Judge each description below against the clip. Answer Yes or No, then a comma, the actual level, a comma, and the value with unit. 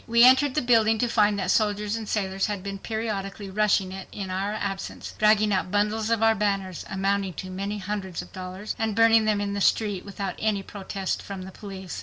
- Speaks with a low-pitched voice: No, high, 205 Hz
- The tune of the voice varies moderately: No, narrow, 2.0 semitones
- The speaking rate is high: Yes, fast, 210 wpm